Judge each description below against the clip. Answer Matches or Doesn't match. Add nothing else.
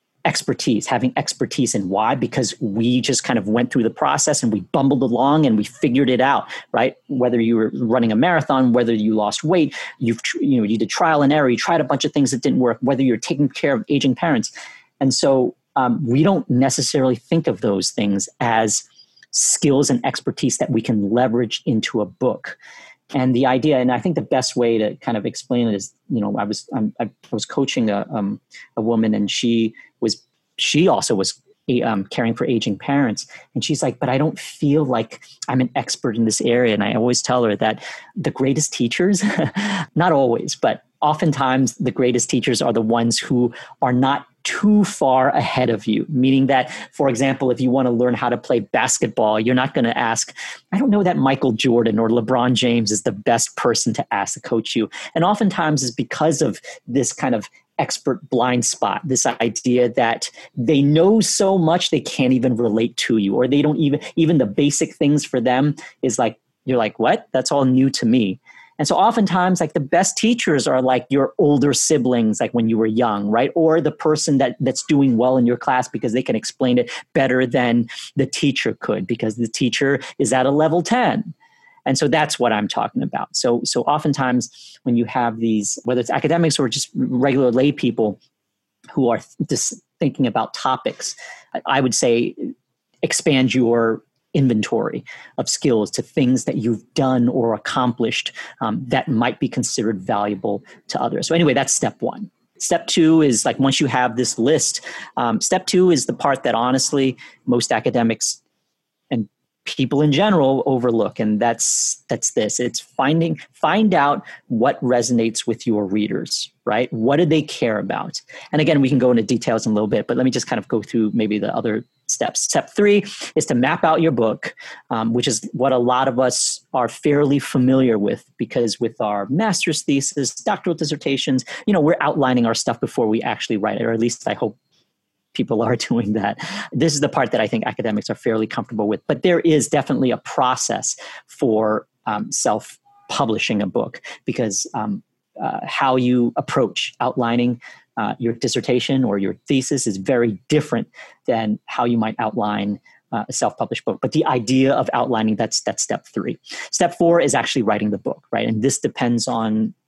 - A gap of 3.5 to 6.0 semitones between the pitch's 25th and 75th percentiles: Matches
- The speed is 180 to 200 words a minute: Matches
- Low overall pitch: Matches